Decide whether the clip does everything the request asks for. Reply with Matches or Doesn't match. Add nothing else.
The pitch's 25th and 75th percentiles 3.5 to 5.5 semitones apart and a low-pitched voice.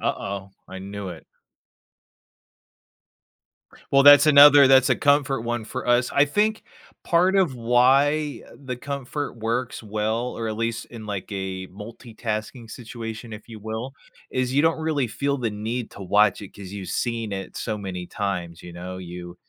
Matches